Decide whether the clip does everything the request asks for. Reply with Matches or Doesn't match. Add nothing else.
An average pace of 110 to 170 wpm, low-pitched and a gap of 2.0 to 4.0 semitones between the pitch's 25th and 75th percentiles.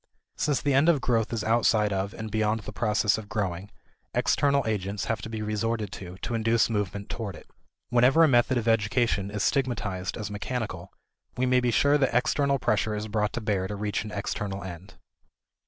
Doesn't match